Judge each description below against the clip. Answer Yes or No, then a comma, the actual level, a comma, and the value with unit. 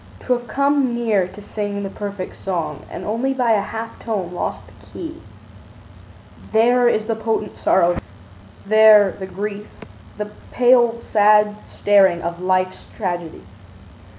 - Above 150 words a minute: No, average, 140 wpm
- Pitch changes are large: No, average, 3.5 semitones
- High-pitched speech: Yes, high, 210 Hz